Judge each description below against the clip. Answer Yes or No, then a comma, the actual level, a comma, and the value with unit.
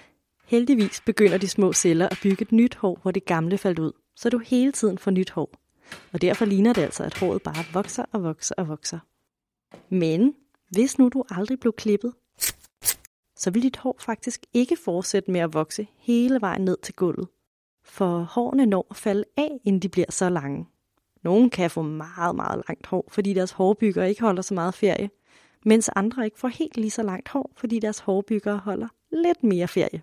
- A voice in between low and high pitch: No, high, 205 Hz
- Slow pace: No, average, 200 wpm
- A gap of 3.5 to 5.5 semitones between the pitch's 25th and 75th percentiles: Yes, average, 4.3 semitones